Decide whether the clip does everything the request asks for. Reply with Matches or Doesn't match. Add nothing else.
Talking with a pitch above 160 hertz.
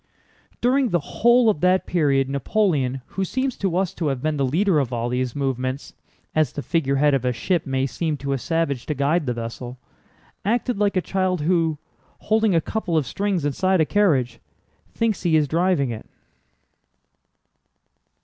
Doesn't match